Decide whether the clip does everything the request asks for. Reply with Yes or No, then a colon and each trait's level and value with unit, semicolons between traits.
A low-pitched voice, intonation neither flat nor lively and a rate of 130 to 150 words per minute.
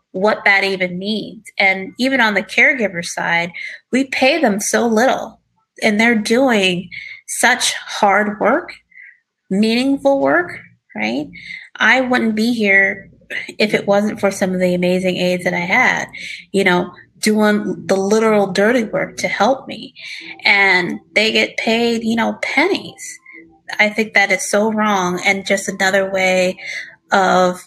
No: high, 210 Hz; average, 4.0 semitones; average, 145 wpm